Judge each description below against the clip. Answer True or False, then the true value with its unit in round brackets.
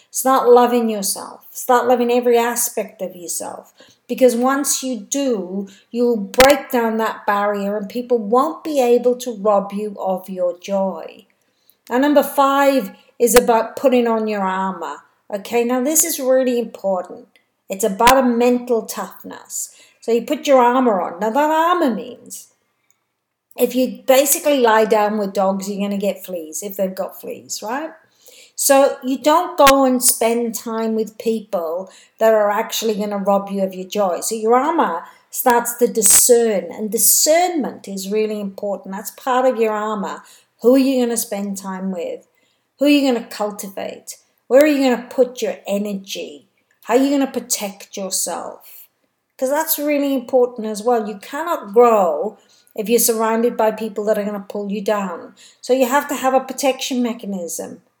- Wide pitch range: False (3.9 semitones)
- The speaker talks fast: False (175 wpm)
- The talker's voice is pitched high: True (235 Hz)